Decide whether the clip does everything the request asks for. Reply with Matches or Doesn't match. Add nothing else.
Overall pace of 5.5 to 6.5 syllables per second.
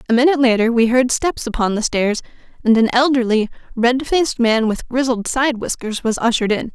Matches